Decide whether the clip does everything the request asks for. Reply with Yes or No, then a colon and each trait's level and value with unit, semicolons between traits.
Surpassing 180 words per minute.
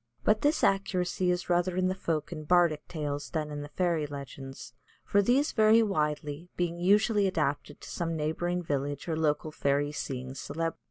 No: average, 175 wpm